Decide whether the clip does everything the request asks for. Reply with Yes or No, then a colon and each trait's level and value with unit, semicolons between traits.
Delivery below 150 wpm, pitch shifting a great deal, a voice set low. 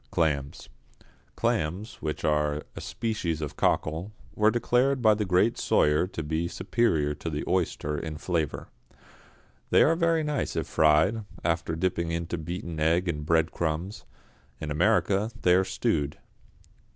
No: average, 140 wpm; average, 5.0 semitones; very low, 85 Hz